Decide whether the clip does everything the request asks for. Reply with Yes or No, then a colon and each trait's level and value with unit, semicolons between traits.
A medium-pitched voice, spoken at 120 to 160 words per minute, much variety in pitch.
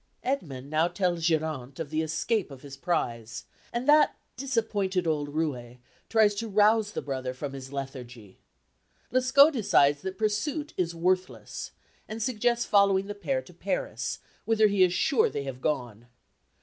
Yes: medium, 180 Hz; average, 155 wpm; wide, 7.9 semitones